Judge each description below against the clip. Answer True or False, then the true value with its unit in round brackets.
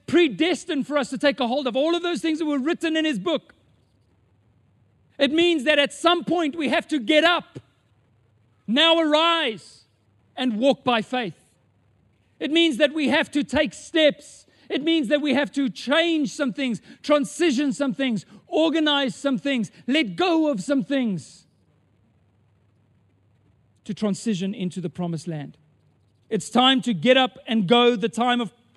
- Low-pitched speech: False (255 Hz)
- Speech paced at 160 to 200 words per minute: True (165 wpm)